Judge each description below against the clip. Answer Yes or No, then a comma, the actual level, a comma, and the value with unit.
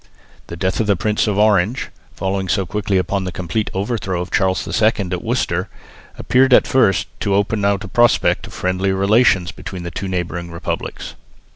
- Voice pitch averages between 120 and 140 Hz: No, very low, 95 Hz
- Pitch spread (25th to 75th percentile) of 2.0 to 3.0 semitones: Yes, narrow, 2.5 semitones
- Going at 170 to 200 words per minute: Yes, average, 180 wpm